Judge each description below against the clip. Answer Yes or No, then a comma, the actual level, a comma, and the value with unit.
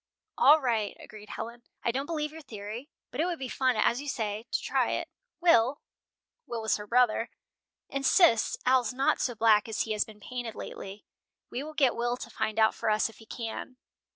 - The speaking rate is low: No, fast, 205 wpm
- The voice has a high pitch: Yes, high, 235 Hz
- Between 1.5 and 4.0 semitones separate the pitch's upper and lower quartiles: Yes, average, 3.5 semitones